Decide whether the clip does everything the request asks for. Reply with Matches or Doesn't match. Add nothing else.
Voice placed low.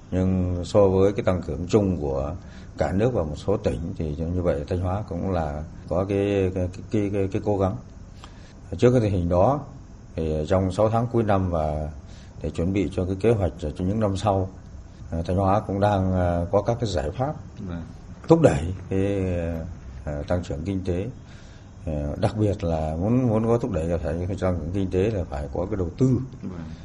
Matches